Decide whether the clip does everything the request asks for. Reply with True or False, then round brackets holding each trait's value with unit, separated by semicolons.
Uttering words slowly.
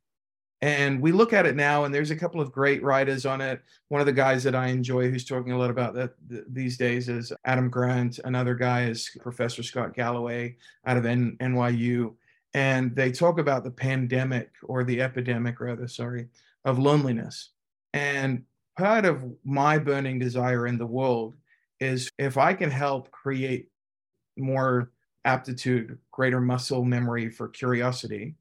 False (165 wpm)